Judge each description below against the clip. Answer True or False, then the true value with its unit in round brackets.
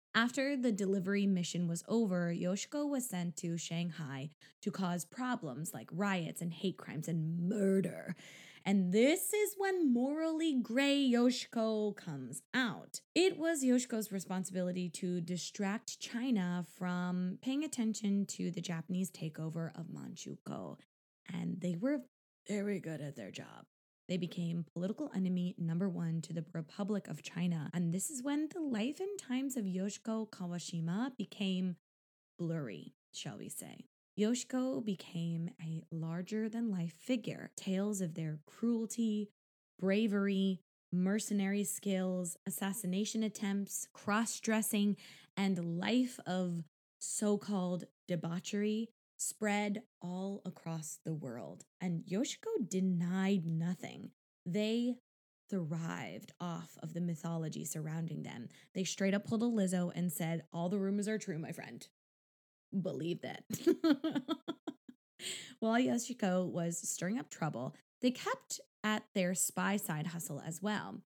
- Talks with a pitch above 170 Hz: True (190 Hz)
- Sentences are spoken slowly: True (130 wpm)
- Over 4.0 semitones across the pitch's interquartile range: True (4.4 semitones)